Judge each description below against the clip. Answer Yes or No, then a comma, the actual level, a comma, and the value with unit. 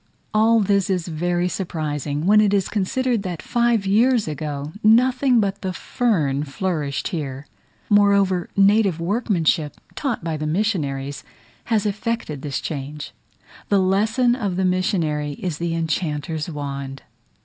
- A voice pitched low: No, medium, 185 Hz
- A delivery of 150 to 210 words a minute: No, slow, 135 wpm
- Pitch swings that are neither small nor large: No, wide, 5.8 semitones